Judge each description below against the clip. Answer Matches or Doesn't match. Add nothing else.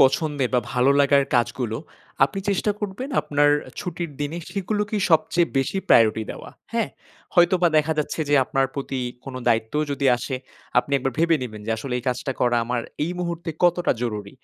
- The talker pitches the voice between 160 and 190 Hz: Doesn't match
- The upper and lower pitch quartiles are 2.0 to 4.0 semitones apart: Doesn't match